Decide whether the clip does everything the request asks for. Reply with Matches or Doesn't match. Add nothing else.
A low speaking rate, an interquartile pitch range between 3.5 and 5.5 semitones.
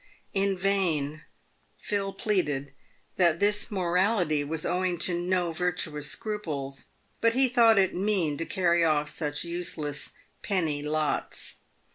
Matches